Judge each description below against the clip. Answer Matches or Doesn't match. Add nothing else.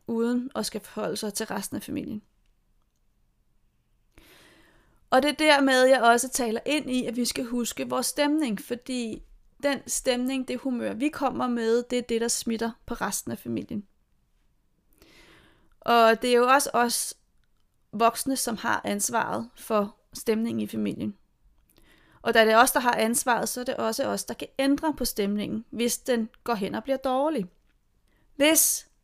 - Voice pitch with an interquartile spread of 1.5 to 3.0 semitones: Matches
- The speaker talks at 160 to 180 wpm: Matches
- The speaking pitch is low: Doesn't match